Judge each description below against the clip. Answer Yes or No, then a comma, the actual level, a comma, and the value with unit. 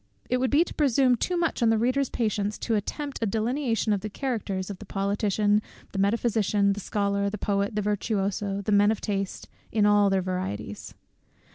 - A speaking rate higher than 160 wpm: Yes, average, 190 wpm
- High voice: Yes, high, 210 Hz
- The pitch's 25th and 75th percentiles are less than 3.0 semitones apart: Yes, narrow, 2.6 semitones